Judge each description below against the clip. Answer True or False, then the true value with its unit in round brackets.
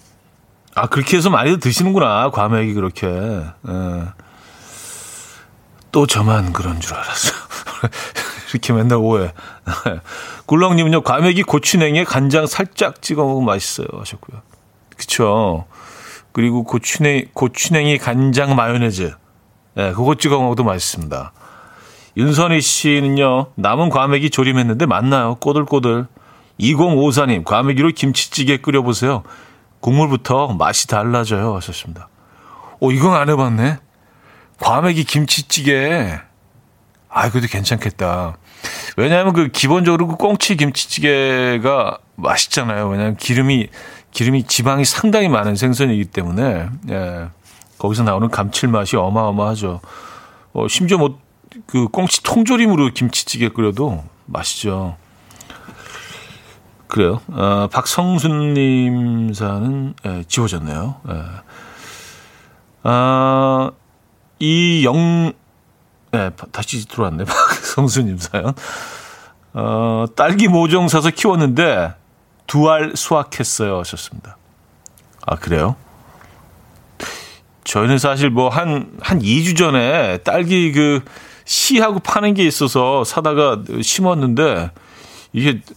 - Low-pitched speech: True (125 Hz)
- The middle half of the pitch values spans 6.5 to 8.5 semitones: False (6.0 semitones)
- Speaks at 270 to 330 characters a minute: False (245 characters per minute)